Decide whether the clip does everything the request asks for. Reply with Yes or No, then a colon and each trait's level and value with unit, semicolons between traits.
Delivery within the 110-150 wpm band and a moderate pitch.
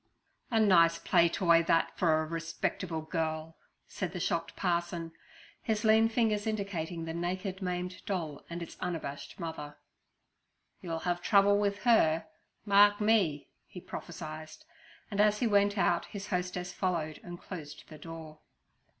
Yes: average, 145 wpm; medium, 175 Hz